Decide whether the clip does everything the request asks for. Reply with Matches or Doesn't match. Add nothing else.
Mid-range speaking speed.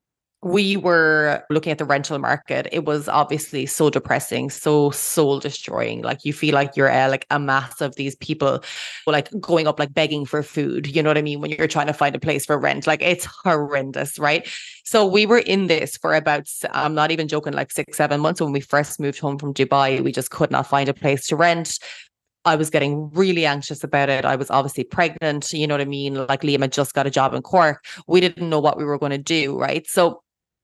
Doesn't match